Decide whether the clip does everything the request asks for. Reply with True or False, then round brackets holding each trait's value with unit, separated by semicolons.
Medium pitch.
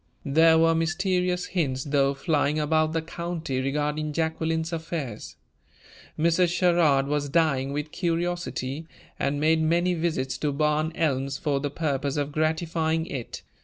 True (155 Hz)